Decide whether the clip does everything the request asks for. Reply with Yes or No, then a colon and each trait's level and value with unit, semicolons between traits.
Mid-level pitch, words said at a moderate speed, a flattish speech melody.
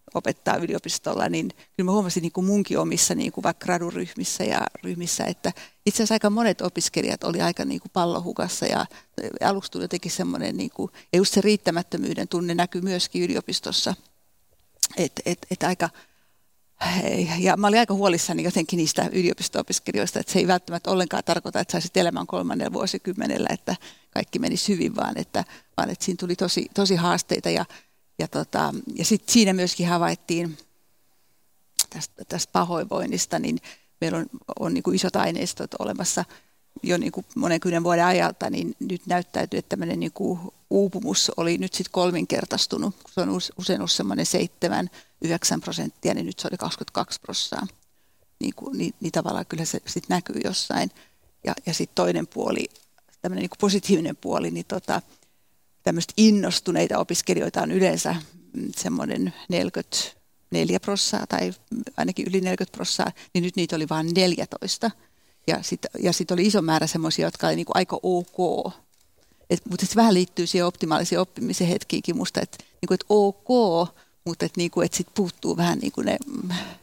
No: medium, 180 Hz; fast, 160 wpm; narrow, 2.2 semitones